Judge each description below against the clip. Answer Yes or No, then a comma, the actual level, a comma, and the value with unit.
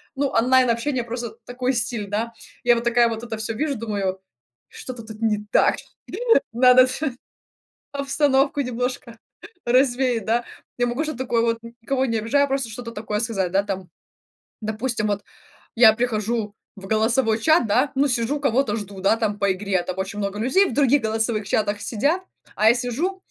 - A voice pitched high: Yes, high, 230 Hz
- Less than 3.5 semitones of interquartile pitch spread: Yes, average, 3.0 semitones